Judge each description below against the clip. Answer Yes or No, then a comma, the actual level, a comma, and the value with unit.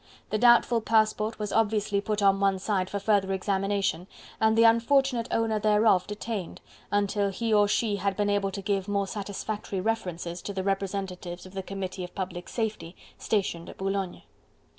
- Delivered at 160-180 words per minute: Yes, average, 170 wpm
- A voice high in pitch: Yes, high, 200 Hz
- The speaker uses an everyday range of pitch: No, narrow, 2.1 semitones